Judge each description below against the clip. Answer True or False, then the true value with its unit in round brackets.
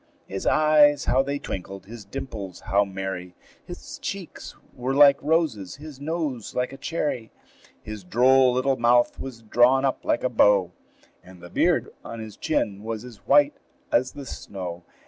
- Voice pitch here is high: False (120 Hz)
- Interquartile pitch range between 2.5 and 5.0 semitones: False (5.6 semitones)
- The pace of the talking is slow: False (165 wpm)